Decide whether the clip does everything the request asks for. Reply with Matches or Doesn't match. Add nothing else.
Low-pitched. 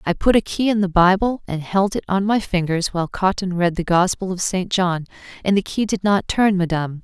Doesn't match